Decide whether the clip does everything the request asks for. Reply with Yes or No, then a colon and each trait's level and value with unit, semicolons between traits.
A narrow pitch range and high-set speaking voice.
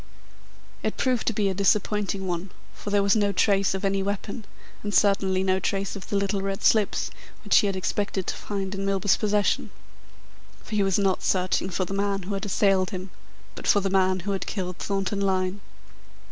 Yes: narrow, 1.2 semitones; high, 195 Hz